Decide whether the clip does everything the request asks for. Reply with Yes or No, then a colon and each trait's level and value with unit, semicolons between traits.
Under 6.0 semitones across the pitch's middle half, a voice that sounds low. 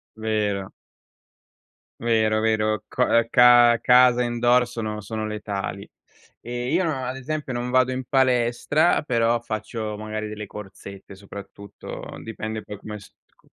Yes: narrow, 2.5 semitones; low, 115 Hz